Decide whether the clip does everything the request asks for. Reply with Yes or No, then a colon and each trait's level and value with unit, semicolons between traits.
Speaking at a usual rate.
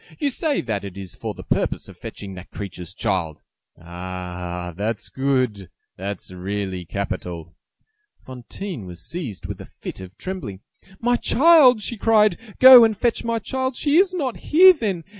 Yes: average, 170 wpm